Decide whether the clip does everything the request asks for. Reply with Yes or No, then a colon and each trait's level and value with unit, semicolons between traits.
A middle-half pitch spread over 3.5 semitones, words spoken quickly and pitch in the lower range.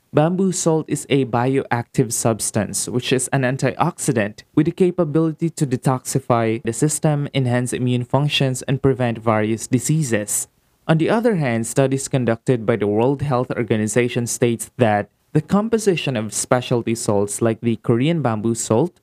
No: average, 4.3 semitones; average, 150 wpm; low, 130 Hz